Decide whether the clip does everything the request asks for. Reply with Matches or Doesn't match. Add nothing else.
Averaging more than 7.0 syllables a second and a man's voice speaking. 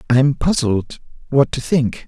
Doesn't match